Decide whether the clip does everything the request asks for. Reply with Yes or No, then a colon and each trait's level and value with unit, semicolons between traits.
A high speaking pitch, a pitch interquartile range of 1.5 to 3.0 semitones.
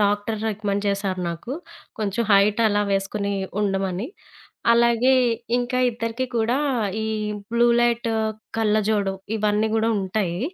Yes: high, 210 Hz; narrow, 2.5 semitones